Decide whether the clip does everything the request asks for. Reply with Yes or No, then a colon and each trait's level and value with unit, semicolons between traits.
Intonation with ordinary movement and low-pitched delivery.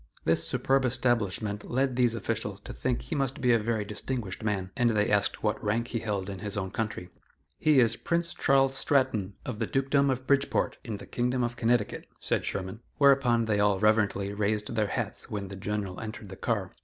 Yes: average, 3.7 semitones; low, 110 Hz